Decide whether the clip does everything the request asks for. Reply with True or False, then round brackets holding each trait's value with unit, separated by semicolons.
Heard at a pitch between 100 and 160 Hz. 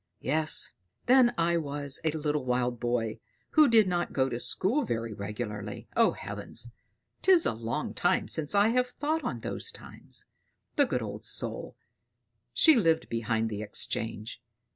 True (140 Hz)